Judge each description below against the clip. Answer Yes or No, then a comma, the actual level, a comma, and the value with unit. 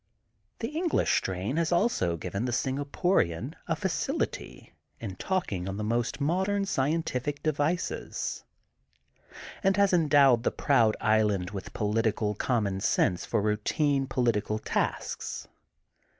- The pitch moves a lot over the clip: Yes, wide, 7.1 semitones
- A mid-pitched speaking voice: No, low, 125 Hz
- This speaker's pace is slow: Yes, slow, 120 wpm